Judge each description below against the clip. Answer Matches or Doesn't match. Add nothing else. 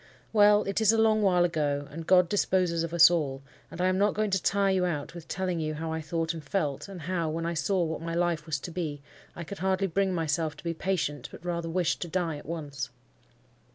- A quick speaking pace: Matches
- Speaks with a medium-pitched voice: Matches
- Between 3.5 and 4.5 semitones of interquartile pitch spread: Doesn't match